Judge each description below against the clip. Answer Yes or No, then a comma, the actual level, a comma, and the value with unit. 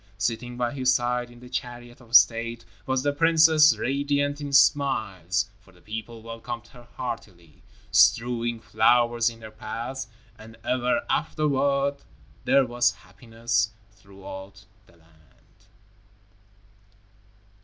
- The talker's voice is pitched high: No, low, 120 Hz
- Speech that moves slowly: Yes, slow, 120 wpm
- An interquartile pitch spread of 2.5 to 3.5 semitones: Yes, average, 2.9 semitones